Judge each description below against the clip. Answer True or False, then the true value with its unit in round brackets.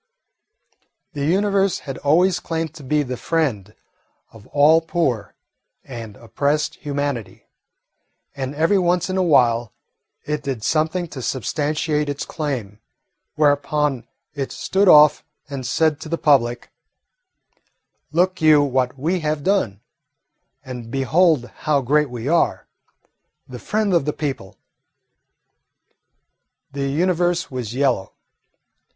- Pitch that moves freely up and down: False (4.0 semitones)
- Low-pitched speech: False (145 Hz)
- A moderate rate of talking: False (120 wpm)